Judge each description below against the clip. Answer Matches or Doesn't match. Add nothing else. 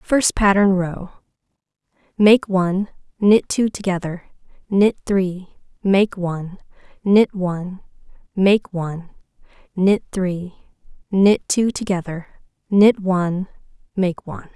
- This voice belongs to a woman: Matches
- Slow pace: Matches